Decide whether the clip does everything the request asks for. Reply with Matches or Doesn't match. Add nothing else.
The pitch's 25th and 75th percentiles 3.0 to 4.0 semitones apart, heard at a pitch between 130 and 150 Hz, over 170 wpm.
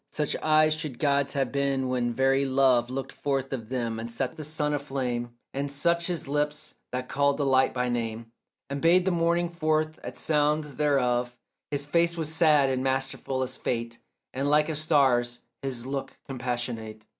Matches